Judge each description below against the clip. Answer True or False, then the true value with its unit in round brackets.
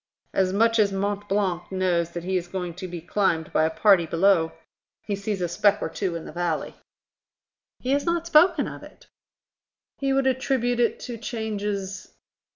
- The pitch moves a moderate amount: True (4.5 semitones)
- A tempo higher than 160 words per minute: True (180 wpm)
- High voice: True (195 Hz)